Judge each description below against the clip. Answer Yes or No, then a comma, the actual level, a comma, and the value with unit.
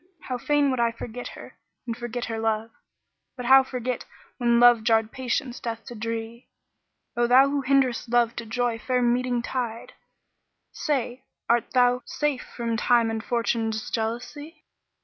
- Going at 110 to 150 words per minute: No, average, 165 wpm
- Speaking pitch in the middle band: No, high, 240 Hz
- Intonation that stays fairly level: Yes, narrow, 1.7 semitones